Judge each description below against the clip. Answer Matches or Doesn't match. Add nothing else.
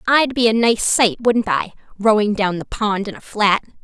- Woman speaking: Matches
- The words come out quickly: Matches